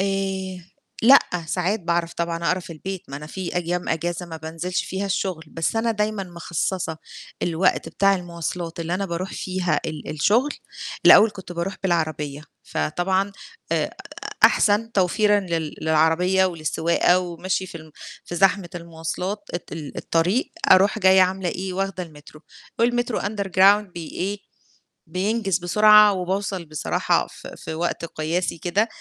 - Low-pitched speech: No, medium, 180 Hz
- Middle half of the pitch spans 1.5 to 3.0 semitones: Yes, average, 2.7 semitones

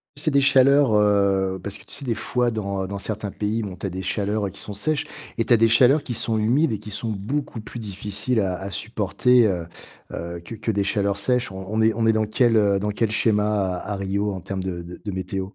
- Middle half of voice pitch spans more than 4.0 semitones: No, average, 2.8 semitones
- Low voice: Yes, low, 105 Hz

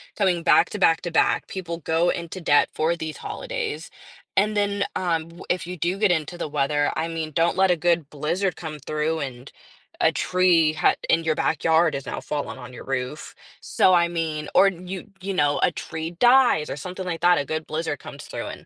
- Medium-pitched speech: Yes, medium, 165 Hz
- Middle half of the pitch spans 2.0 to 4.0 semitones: Yes, average, 2.9 semitones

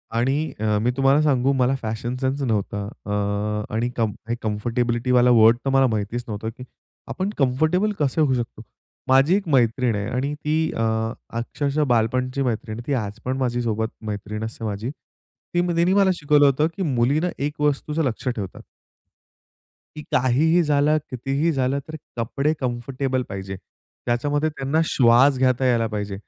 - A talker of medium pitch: No, low, 130 Hz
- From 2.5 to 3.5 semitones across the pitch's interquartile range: No, average, 3.9 semitones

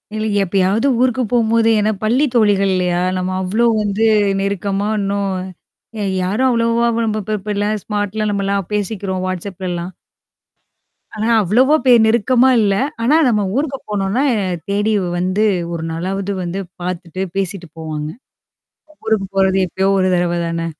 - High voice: Yes, high, 200 Hz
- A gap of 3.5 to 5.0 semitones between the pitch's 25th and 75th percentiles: No, average, 2.8 semitones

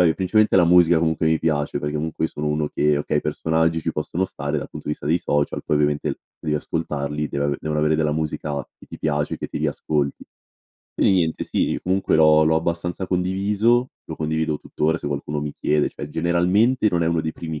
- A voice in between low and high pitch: No, very low, 80 Hz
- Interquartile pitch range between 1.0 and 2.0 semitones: No, narrow, 2.5 semitones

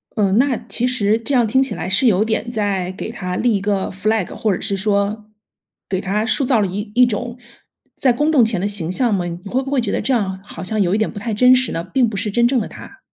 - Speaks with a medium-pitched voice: No, high, 215 Hz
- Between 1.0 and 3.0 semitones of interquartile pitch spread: No, average, 3.7 semitones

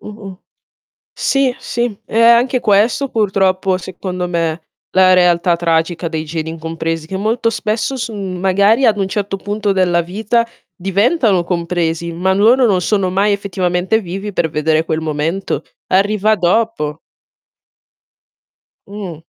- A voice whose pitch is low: No, high, 190 Hz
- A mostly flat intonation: No, average, 3.7 semitones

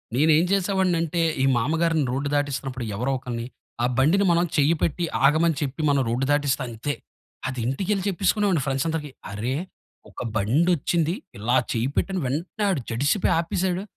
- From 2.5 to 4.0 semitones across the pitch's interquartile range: No, average, 4.6 semitones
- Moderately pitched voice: Yes, medium, 150 Hz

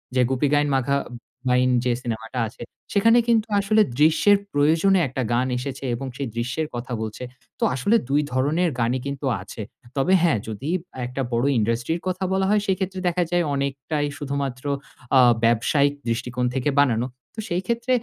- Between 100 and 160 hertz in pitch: Yes, medium, 140 Hz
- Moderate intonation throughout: No, wide, 5.8 semitones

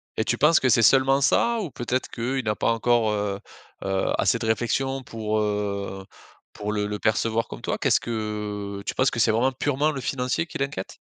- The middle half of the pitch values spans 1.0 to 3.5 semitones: No, average, 4.1 semitones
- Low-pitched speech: Yes, low, 115 Hz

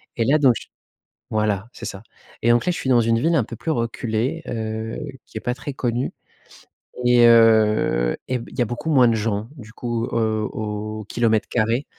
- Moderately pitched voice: No, low, 115 Hz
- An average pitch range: No, narrow, 2.1 semitones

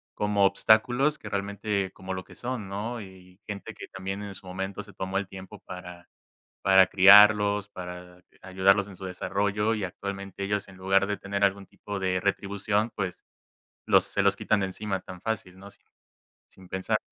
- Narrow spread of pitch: Yes, narrow, 1.6 semitones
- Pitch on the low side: Yes, low, 100 Hz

